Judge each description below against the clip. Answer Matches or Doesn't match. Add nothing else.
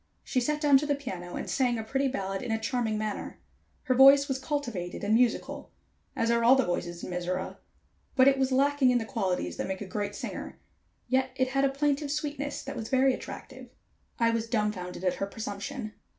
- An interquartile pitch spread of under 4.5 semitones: Doesn't match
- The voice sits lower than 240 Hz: Doesn't match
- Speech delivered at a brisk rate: Matches